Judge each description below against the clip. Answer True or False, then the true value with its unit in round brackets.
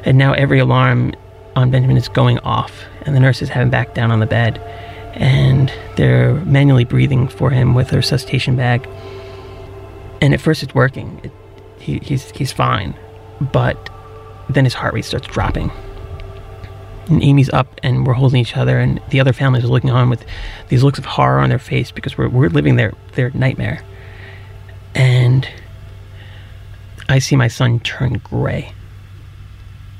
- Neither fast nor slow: True (165 wpm)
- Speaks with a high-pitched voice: False (120 Hz)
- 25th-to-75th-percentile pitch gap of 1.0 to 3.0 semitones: False (5.1 semitones)